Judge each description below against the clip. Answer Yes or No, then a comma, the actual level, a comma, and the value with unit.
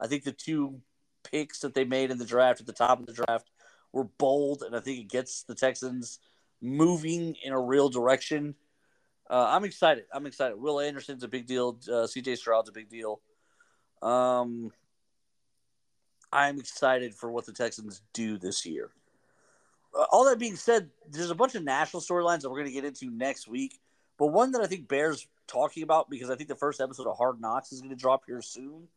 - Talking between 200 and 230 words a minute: Yes, fast, 205 wpm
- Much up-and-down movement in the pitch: No, average, 3.7 semitones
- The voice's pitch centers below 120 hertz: No, low, 135 Hz